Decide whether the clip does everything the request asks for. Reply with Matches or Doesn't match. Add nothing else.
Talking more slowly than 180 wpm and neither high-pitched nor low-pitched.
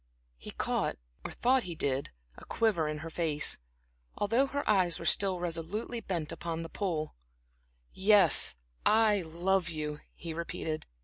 Matches